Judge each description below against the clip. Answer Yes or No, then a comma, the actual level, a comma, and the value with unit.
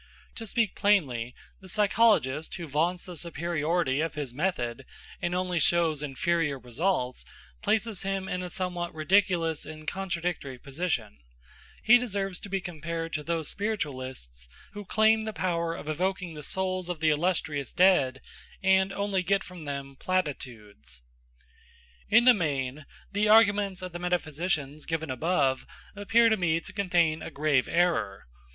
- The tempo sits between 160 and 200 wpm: No, average, 145 wpm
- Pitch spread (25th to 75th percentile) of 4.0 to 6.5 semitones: Yes, average, 4.6 semitones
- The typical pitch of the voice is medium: Yes, medium, 170 Hz